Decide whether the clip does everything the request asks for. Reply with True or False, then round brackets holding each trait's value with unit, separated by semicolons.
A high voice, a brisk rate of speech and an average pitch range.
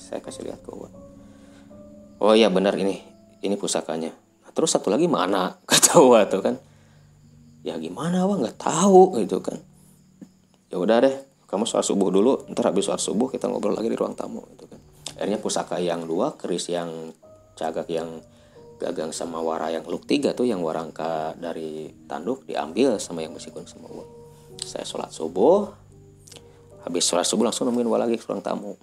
False (85 Hz; 170 wpm; 4.2 semitones)